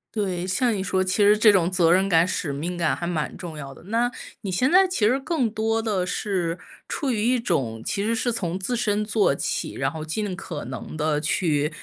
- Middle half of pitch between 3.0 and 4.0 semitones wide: No, average, 5.2 semitones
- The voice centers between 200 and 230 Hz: No, high, 190 Hz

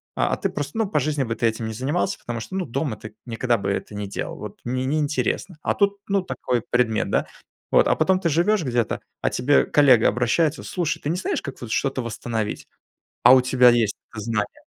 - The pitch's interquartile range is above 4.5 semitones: Yes, average, 5.2 semitones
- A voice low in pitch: Yes, low, 130 Hz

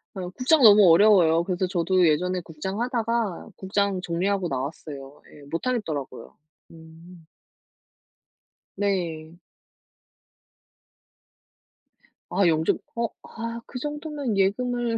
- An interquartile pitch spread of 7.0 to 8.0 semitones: No, wide, 5.6 semitones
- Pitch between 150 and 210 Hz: Yes, medium, 185 Hz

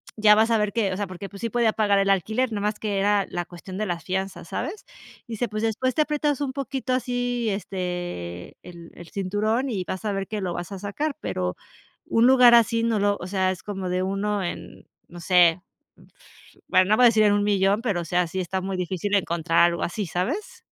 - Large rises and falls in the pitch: No, average, 3.6 semitones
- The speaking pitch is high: Yes, high, 200 Hz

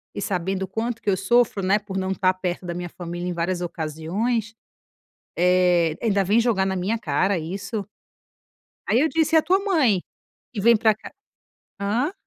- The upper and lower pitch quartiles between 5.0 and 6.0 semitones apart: No, average, 4.1 semitones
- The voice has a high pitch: Yes, high, 195 Hz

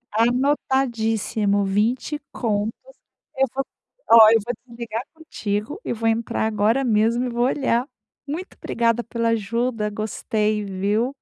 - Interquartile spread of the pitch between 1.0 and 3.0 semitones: Yes, average, 2.7 semitones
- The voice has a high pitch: Yes, high, 230 Hz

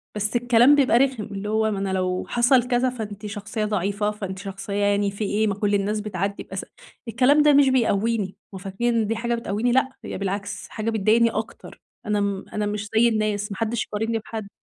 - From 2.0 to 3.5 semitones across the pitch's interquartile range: Yes, narrow, 2.5 semitones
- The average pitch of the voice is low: No, high, 215 Hz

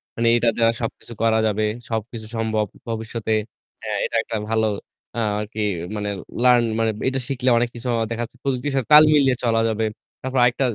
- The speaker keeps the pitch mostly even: Yes, narrow, 2.1 semitones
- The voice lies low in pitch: Yes, low, 115 Hz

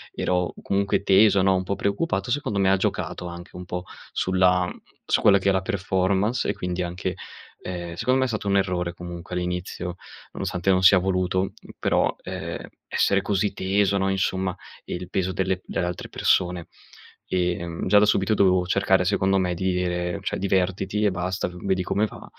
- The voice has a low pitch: Yes, very low, 95 Hz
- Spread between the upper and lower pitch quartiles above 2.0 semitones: No, narrow, 1.7 semitones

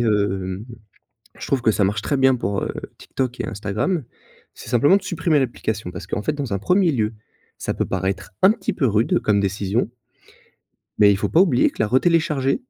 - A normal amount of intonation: No, wide, 6.0 semitones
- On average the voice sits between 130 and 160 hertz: No, low, 115 Hz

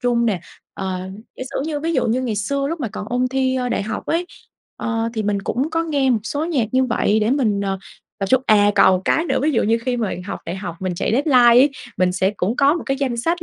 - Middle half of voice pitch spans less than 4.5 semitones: No, average, 5.0 semitones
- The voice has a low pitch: No, high, 240 Hz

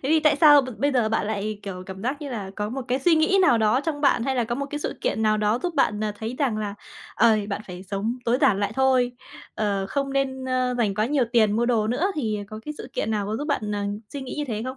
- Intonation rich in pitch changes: No, average, 4.5 semitones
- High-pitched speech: Yes, high, 235 Hz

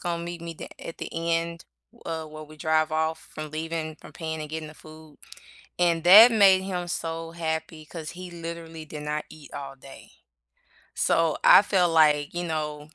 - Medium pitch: Yes, medium, 160 Hz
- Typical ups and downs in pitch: No, narrow, 1.5 semitones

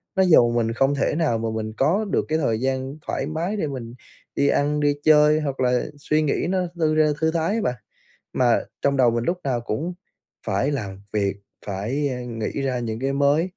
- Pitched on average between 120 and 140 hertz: Yes, low, 135 Hz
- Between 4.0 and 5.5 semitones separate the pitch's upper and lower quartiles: Yes, average, 4.6 semitones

